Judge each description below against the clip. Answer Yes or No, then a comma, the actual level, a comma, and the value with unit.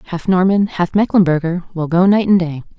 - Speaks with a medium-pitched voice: Yes, medium, 180 Hz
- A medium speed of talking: Yes, average, 195 wpm